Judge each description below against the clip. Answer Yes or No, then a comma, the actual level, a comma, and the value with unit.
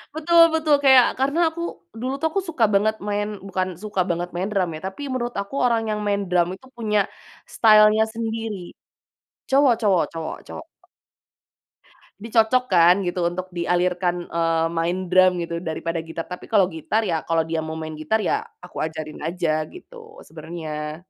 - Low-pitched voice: No, medium, 185 Hz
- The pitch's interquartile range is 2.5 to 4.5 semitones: No, average, 5.1 semitones